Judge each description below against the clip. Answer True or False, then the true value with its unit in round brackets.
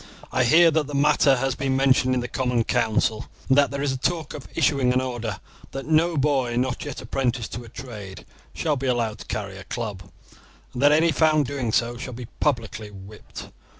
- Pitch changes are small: False (3.3 semitones)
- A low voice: True (130 Hz)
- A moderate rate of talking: False (210 wpm)